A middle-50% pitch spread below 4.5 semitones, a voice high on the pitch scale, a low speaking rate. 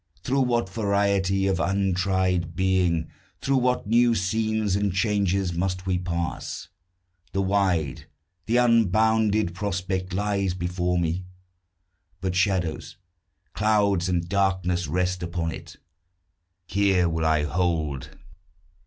No: narrow, 2.5 semitones; very low, 95 Hz; slow, 110 wpm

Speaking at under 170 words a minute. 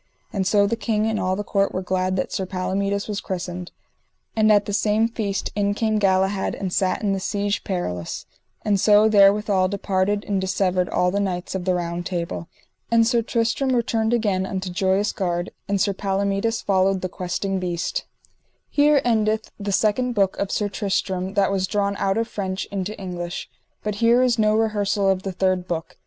No: average, 190 wpm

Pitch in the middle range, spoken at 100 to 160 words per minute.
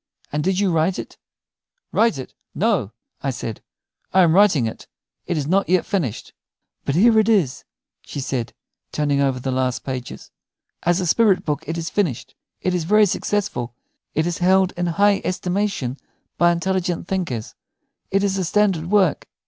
No: medium, 175 Hz; average, 170 wpm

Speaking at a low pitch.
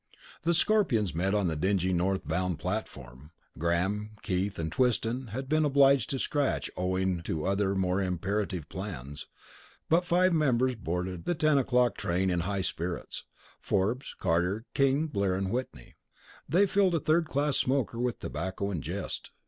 Yes: low, 100 Hz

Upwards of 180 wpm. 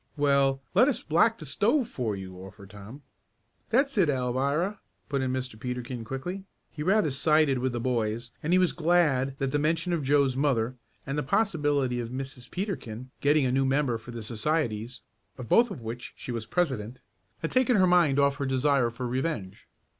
Yes: average, 190 wpm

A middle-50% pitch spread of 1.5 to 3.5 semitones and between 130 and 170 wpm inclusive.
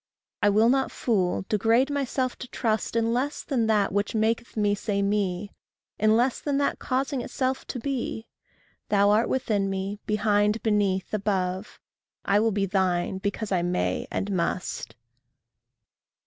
Yes: average, 3.1 semitones; average, 150 wpm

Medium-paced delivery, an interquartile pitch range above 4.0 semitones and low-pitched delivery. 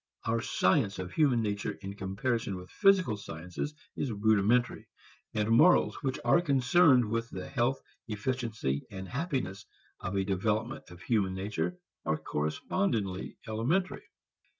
No: slow, 130 wpm; average, 5.1 semitones; low, 110 Hz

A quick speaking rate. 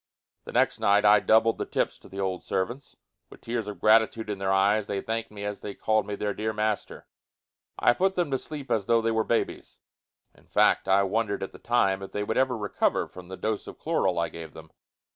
Yes: fast, 230 wpm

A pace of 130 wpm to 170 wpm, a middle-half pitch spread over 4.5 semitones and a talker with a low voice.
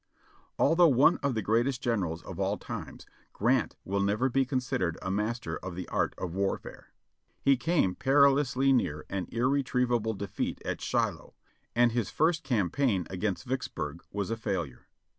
Yes: average, 160 wpm; wide, 5.4 semitones; low, 120 Hz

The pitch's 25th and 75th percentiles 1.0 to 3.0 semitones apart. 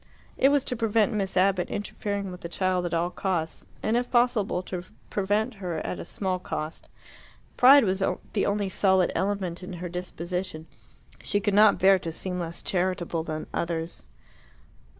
Yes: narrow, 2.6 semitones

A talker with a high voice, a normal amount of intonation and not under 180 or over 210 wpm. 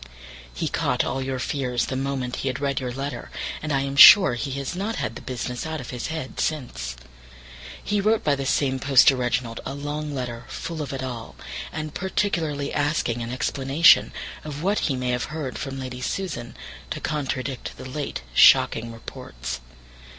No: low, 135 Hz; average, 3.3 semitones; average, 185 wpm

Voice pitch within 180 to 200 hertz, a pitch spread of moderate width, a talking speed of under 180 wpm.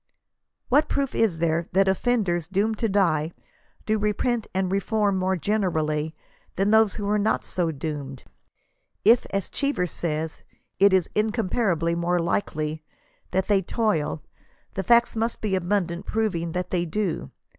Yes: high, 190 Hz; average, 4.2 semitones; average, 150 wpm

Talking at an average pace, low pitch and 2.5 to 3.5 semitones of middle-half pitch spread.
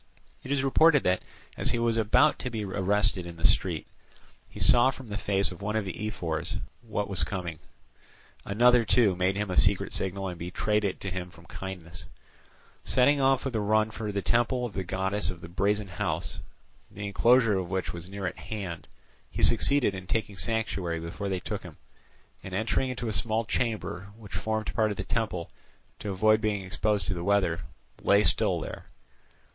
Yes: average, 195 wpm; low, 100 Hz; average, 3.2 semitones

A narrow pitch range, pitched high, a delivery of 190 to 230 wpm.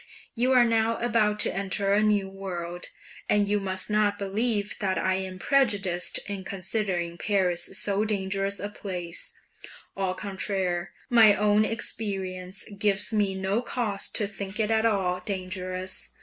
No: narrow, 2.0 semitones; high, 200 Hz; average, 150 wpm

